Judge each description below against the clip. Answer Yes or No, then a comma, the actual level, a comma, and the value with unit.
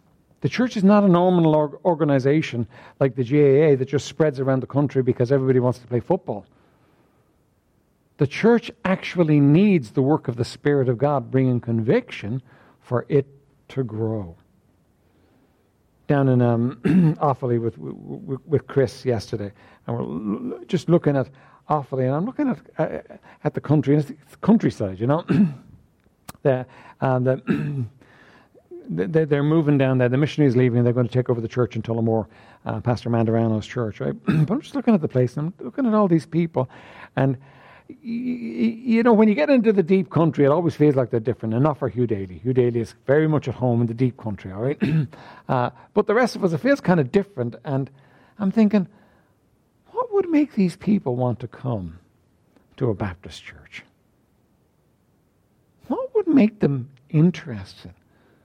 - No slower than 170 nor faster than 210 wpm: Yes, average, 180 wpm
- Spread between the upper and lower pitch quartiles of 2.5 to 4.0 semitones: No, wide, 5.5 semitones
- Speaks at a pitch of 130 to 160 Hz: Yes, low, 135 Hz